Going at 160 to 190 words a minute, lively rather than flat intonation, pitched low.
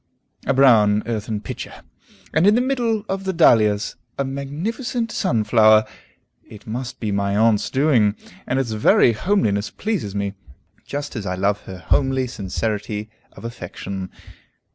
No: average, 140 wpm; wide, 5.7 semitones; low, 115 Hz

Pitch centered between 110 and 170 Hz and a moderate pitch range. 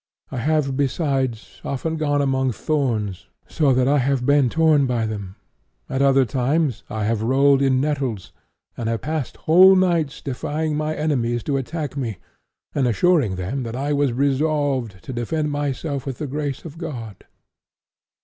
Yes: low, 135 Hz; average, 3.5 semitones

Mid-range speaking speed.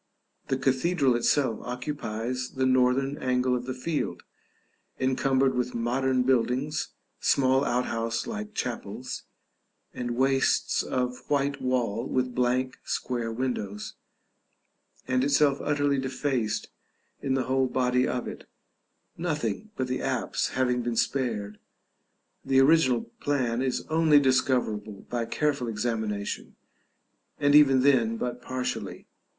No: slow, 120 wpm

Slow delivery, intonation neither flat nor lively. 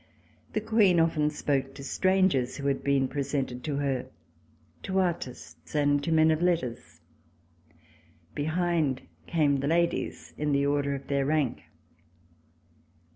Yes: slow, 130 wpm; average, 3.2 semitones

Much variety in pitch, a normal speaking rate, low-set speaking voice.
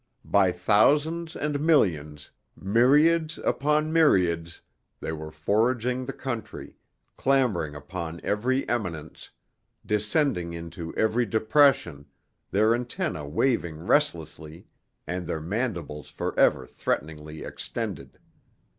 No: wide, 8.4 semitones; slow, 95 wpm; low, 105 Hz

